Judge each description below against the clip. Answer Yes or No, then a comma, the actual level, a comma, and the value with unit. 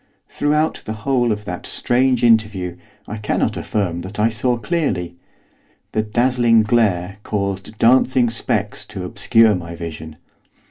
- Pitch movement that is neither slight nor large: Yes, average, 3.7 semitones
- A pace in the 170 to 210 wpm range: No, slow, 135 wpm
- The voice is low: Yes, low, 110 Hz